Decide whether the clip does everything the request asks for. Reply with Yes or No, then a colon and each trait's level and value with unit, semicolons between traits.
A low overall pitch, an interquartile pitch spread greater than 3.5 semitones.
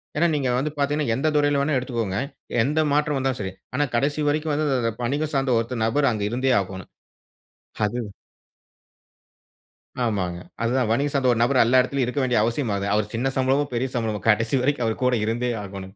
Yes: low, 125 Hz; average, 4.0 semitones